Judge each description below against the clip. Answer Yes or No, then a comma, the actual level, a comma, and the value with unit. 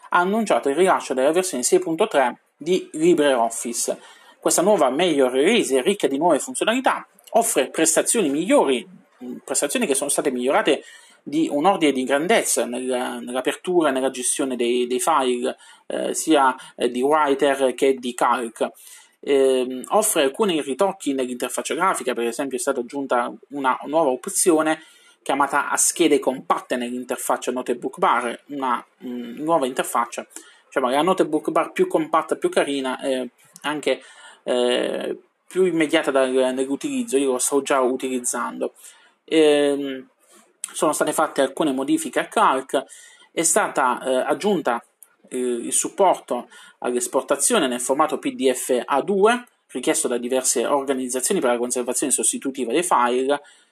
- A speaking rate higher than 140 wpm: No, average, 135 wpm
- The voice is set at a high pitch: No, medium, 140 Hz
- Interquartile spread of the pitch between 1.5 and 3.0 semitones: No, wide, 5.6 semitones